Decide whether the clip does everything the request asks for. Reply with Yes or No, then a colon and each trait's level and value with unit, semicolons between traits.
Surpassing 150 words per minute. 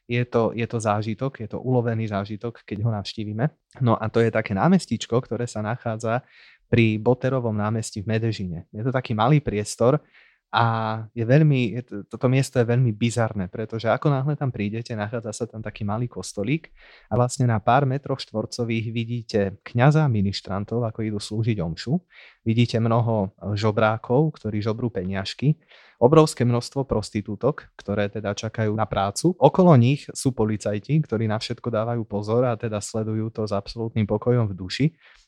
Yes: average, 160 wpm